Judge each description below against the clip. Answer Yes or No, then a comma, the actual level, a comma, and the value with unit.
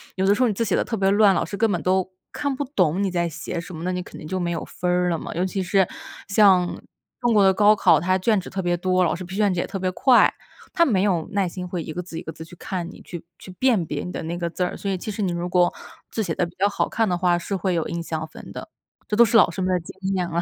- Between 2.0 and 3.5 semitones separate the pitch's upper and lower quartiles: Yes, narrow, 2.4 semitones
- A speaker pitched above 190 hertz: No, medium, 185 Hz